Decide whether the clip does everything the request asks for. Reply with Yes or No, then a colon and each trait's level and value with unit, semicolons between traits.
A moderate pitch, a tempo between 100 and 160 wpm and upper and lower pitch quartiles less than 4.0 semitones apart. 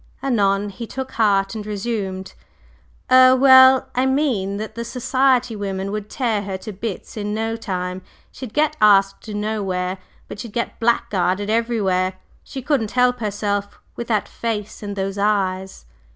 No: high, 210 Hz; average, 150 wpm; average, 3.4 semitones